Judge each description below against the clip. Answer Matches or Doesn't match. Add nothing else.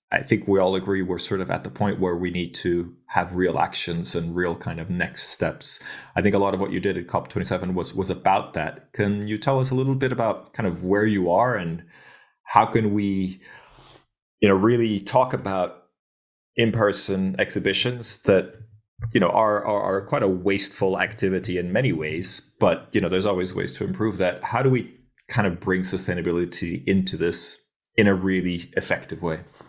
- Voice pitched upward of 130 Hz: Doesn't match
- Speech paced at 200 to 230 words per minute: Matches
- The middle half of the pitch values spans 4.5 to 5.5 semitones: Doesn't match